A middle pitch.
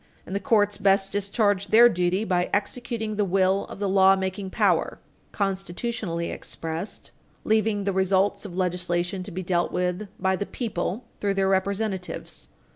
No: high, 195 Hz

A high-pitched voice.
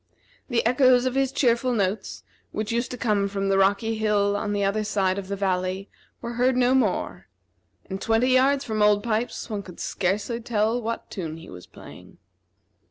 Yes: high, 215 Hz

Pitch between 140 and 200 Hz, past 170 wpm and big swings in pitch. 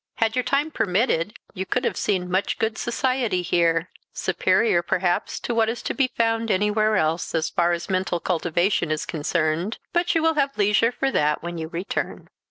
No: high, 190 Hz; average, 185 wpm; average, 5.0 semitones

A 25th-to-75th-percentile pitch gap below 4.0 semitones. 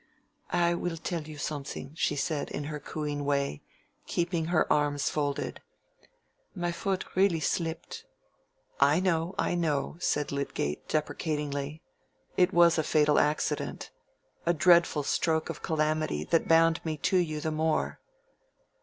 Yes: narrow, 2.5 semitones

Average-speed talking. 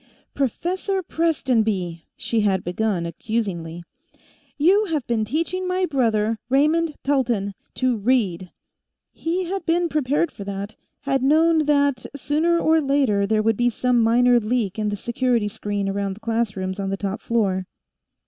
Yes: average, 150 wpm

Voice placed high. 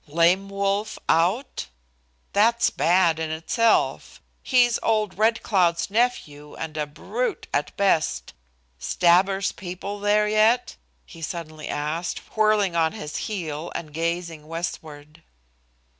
No: medium, 180 Hz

